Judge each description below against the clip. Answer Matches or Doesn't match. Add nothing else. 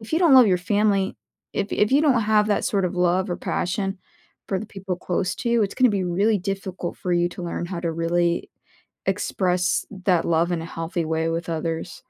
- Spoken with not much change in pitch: Doesn't match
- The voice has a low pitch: Doesn't match